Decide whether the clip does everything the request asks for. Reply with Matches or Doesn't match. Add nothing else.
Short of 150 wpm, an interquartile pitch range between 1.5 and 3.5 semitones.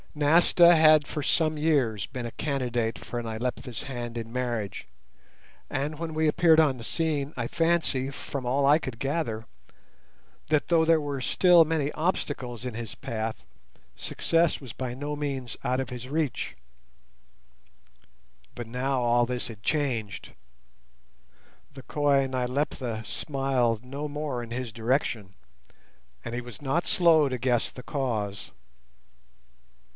Doesn't match